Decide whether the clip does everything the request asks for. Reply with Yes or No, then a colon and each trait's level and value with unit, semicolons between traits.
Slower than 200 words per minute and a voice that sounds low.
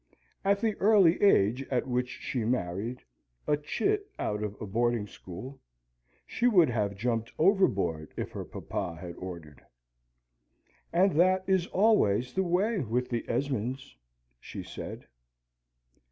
Yes: slow, 135 wpm; low, 125 Hz